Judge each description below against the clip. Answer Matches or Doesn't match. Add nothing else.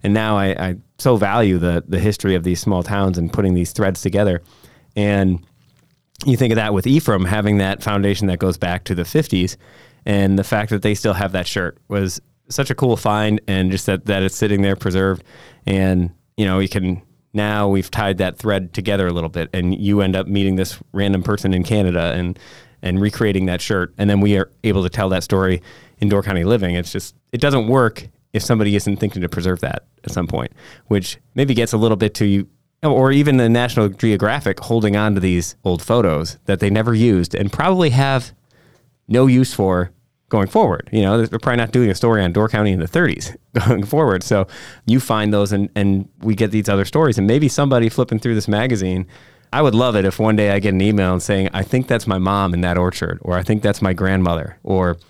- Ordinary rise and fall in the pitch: Matches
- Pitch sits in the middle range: Doesn't match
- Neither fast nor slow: Doesn't match